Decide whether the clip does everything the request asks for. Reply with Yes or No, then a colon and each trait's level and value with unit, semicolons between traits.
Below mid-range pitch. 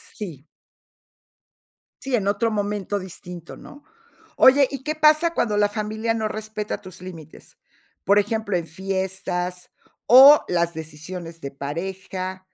No: high, 195 Hz